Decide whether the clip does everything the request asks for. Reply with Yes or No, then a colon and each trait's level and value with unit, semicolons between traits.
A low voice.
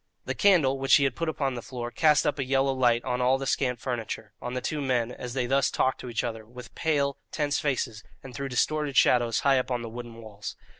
Yes: low, 130 Hz